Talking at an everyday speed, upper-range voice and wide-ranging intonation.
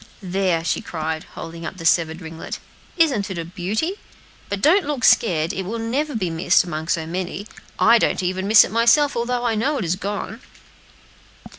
Yes: average, 185 wpm; high, 195 Hz; wide, 5.8 semitones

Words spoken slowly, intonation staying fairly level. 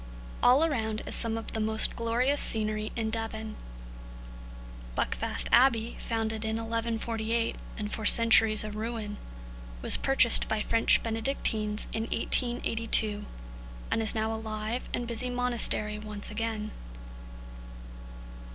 Yes: slow, 125 wpm; narrow, 1.2 semitones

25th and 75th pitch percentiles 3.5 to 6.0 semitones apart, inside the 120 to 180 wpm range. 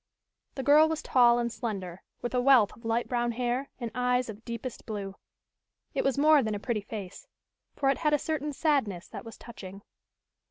No: average, 3.8 semitones; average, 195 wpm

